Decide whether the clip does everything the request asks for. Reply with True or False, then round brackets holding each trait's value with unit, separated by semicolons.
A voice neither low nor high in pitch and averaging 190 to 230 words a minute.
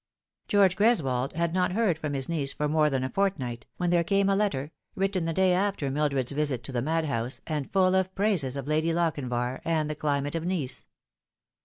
True (155 Hz; 200 wpm)